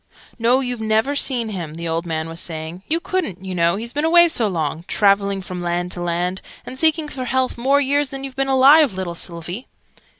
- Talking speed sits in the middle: No, fast, 210 wpm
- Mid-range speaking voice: No, high, 215 Hz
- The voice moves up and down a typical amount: No, wide, 7.5 semitones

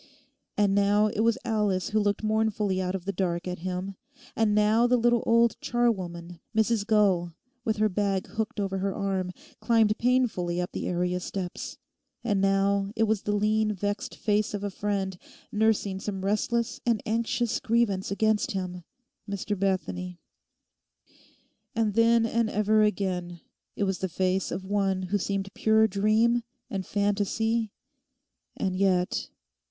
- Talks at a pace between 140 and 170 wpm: Yes, average, 150 wpm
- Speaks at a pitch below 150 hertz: No, high, 205 Hz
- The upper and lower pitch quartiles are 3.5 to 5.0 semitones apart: No, narrow, 2.5 semitones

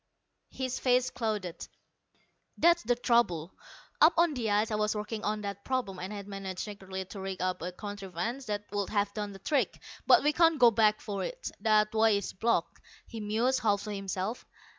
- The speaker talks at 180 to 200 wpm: Yes, average, 190 wpm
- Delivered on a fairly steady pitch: No, average, 3.3 semitones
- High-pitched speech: Yes, high, 210 Hz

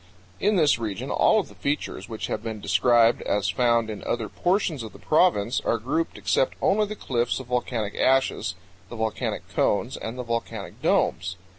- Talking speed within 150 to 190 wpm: Yes, average, 180 wpm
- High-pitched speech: No, low, 120 Hz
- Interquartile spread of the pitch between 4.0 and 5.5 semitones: No, average, 3.6 semitones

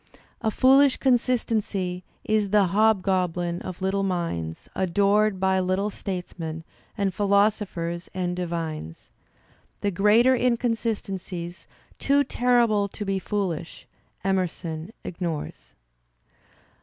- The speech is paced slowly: Yes, slow, 95 wpm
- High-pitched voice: Yes, high, 195 Hz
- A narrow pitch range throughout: No, average, 3.4 semitones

